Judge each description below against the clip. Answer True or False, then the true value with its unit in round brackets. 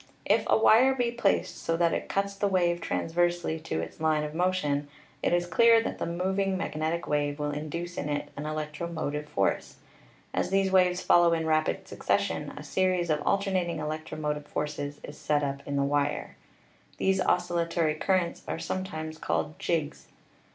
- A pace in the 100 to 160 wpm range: False (175 wpm)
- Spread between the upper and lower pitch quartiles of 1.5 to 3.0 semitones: False (3.5 semitones)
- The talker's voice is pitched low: False (165 Hz)